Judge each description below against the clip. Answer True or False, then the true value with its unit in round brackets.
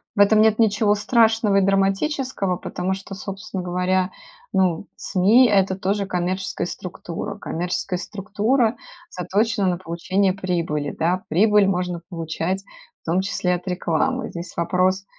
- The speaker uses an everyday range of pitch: False (2.3 semitones)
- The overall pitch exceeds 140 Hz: True (190 Hz)